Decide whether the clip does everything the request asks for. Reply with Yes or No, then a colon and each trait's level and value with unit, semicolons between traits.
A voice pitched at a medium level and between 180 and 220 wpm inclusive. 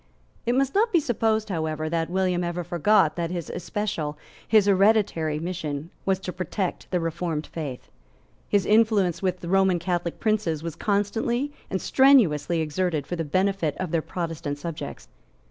No: medium, 180 Hz; average, 155 wpm